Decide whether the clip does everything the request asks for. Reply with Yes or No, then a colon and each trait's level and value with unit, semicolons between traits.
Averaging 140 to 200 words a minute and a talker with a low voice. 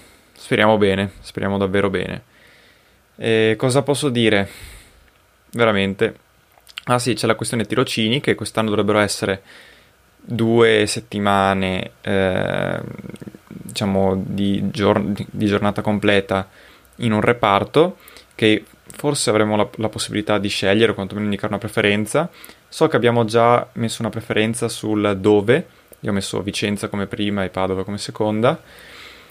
No: average, 130 wpm; low, 105 Hz